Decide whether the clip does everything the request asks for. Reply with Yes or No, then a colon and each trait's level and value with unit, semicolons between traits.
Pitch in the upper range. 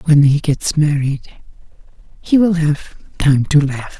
No: medium, 150 Hz